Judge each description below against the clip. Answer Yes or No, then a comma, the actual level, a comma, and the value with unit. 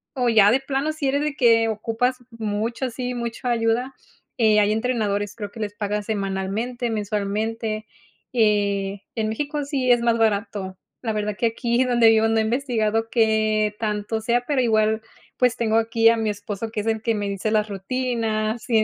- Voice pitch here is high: Yes, high, 225 Hz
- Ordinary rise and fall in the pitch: No, narrow, 2.2 semitones